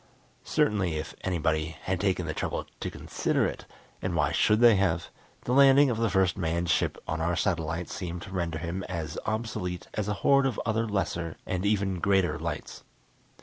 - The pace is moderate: Yes, average, 185 wpm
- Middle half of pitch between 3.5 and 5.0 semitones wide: Yes, average, 4.1 semitones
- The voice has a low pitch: Yes, very low, 95 Hz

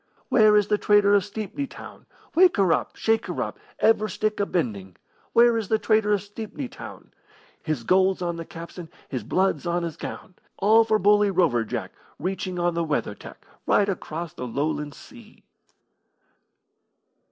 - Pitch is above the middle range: Yes, high, 195 Hz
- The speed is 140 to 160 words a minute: No, average, 170 wpm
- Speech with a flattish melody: No, average, 4.3 semitones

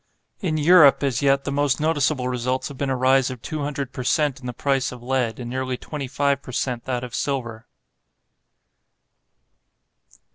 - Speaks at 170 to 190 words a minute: Yes, average, 180 wpm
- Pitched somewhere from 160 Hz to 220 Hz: No, low, 135 Hz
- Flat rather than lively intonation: Yes, narrow, 2.2 semitones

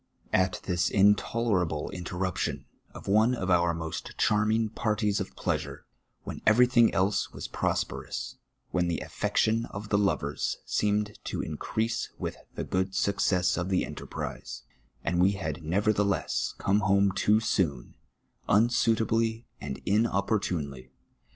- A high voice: No, low, 100 Hz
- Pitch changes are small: No, average, 3.2 semitones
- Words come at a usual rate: No, slow, 130 wpm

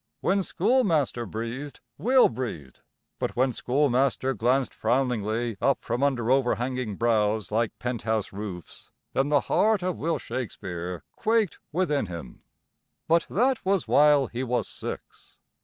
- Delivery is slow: Yes, slow, 130 wpm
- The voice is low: Yes, low, 125 Hz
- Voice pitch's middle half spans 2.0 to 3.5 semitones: No, average, 5.0 semitones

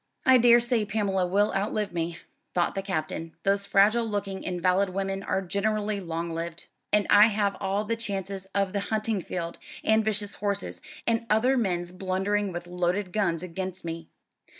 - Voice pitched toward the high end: Yes, high, 195 Hz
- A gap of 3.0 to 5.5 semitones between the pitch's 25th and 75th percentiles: No, narrow, 2.6 semitones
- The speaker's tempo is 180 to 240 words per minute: No, average, 165 wpm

